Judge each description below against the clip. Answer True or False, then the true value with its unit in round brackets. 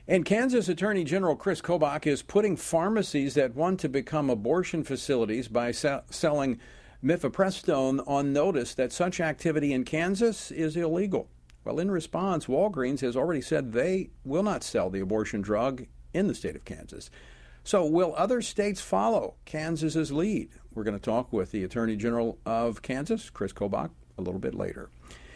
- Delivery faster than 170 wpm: False (165 wpm)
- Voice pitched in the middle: True (150 Hz)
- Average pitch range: False (7.0 semitones)